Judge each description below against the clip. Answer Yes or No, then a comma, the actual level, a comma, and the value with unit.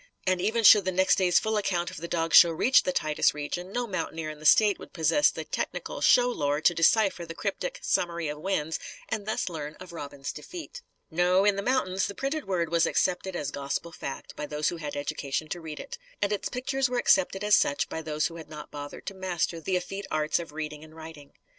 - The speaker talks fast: Yes, fast, 230 wpm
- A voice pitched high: No, medium, 175 Hz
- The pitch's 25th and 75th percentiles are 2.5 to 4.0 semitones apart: No, average, 4.5 semitones